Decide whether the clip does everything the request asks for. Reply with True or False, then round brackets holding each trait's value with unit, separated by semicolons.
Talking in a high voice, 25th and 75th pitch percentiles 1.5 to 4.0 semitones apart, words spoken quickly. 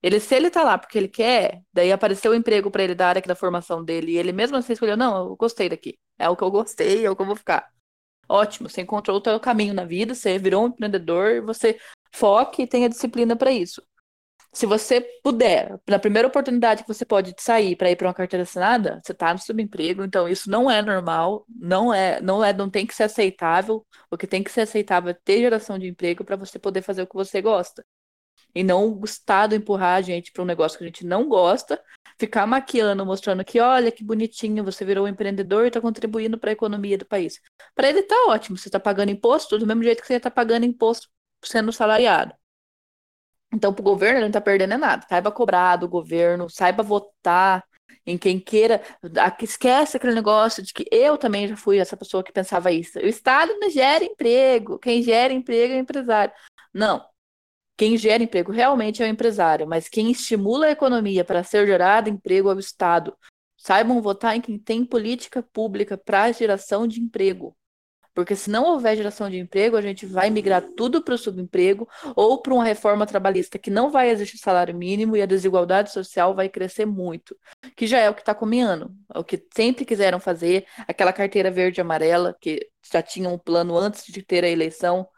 True (205 Hz; 3.6 semitones; 210 wpm)